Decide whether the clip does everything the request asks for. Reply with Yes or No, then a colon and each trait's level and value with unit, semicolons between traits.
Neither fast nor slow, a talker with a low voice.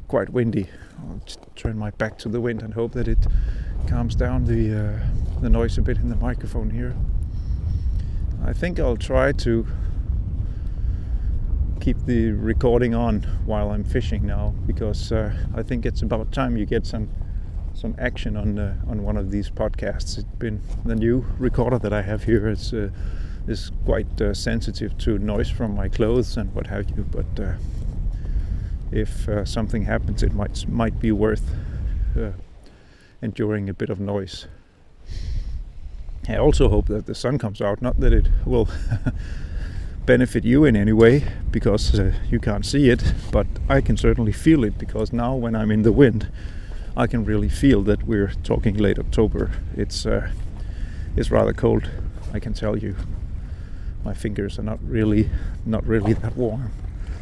Yes: average, 170 wpm; low, 105 Hz